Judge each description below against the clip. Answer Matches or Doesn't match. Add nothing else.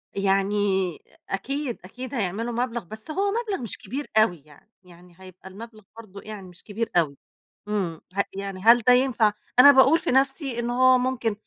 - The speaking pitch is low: Doesn't match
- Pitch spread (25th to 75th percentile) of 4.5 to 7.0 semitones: Matches